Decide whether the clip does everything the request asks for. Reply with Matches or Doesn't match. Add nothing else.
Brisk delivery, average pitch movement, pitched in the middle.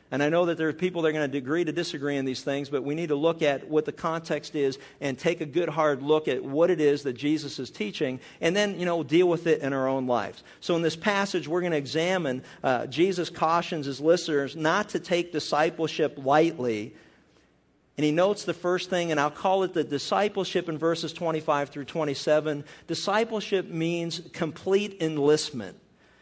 Matches